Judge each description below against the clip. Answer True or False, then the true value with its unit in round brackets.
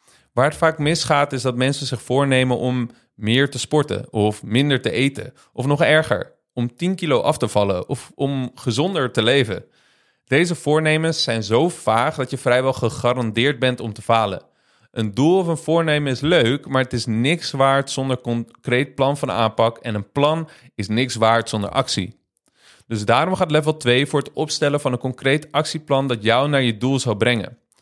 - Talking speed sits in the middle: True (190 wpm)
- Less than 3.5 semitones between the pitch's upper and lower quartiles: False (3.8 semitones)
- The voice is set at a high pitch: False (130 Hz)